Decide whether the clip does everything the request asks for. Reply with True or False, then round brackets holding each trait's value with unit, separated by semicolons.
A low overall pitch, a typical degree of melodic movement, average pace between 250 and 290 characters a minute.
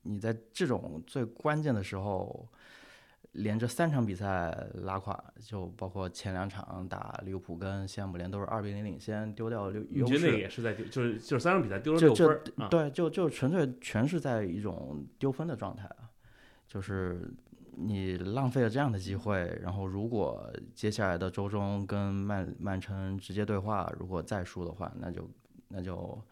True (105 Hz; 3.9 semitones; 260 characters per minute)